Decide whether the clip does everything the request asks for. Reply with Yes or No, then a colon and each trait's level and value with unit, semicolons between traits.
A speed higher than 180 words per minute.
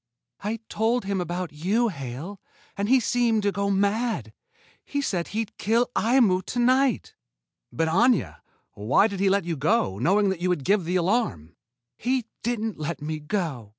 No: average, 175 wpm